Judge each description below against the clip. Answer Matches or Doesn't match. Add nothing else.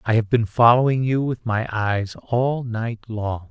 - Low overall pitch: Matches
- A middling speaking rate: Matches